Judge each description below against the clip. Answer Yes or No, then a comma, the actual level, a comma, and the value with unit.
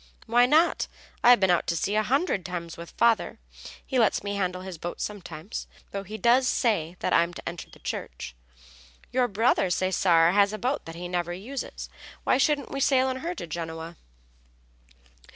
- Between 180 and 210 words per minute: Yes, average, 185 wpm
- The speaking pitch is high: Yes, high, 200 Hz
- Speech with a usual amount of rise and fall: No, wide, 6.0 semitones